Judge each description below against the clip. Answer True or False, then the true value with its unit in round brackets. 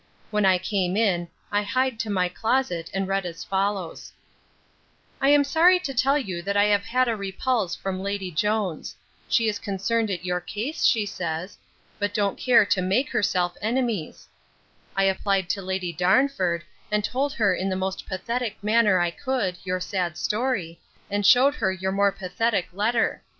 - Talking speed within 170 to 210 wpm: True (175 wpm)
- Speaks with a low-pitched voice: False (200 Hz)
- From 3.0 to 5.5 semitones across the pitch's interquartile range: True (3.8 semitones)